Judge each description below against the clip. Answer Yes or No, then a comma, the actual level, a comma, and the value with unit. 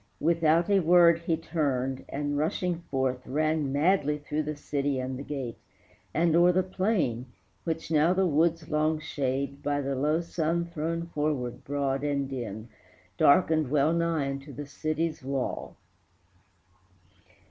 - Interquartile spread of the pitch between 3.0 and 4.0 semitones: Yes, average, 3.3 semitones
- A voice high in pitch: No, medium, 150 Hz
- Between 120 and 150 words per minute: Yes, average, 140 wpm